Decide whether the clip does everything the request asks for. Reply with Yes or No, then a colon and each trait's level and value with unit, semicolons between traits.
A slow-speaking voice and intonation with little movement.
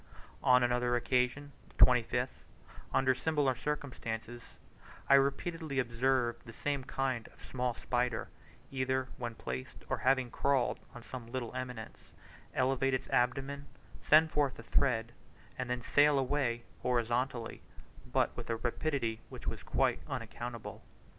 Yes: slow, 130 wpm; narrow, 2.1 semitones